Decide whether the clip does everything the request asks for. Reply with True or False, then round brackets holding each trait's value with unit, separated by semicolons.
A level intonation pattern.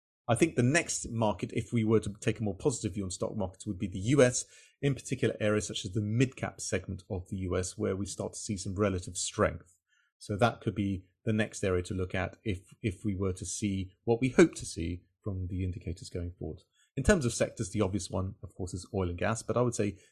False (3.3 semitones)